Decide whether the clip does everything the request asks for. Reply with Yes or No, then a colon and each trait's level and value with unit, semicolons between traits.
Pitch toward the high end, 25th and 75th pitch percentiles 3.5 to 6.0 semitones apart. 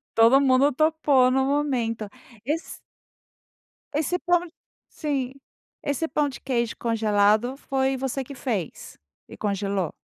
Yes: very high, 265 Hz; average, 4.0 semitones